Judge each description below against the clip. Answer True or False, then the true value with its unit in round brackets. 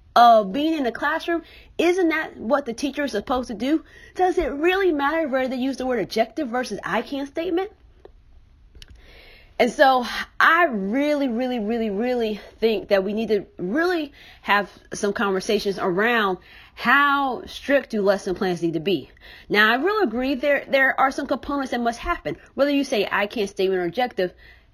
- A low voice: False (255 Hz)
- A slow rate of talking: False (180 wpm)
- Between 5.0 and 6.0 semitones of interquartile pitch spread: True (5.6 semitones)